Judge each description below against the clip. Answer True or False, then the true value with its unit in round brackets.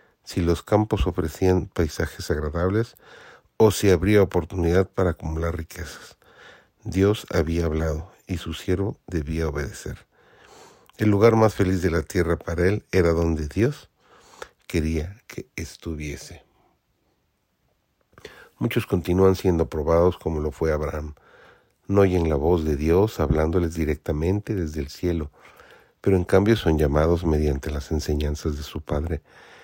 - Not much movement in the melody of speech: False (3.3 semitones)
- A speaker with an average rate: True (135 wpm)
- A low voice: True (85 Hz)